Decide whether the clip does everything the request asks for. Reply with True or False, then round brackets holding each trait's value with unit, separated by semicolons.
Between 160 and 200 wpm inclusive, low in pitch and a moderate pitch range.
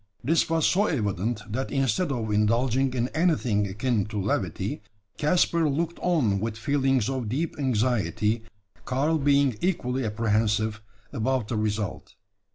False (135 wpm; 125 Hz; 4.8 semitones)